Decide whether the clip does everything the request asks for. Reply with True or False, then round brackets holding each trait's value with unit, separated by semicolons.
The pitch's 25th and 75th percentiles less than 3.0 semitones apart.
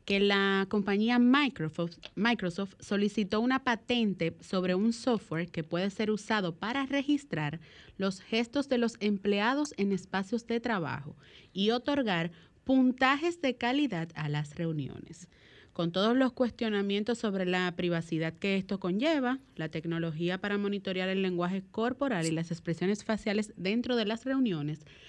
False (5.3 semitones)